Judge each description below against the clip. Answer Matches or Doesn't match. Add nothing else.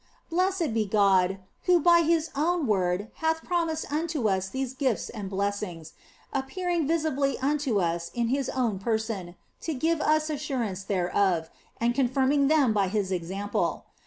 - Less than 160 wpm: Matches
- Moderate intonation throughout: Doesn't match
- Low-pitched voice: Doesn't match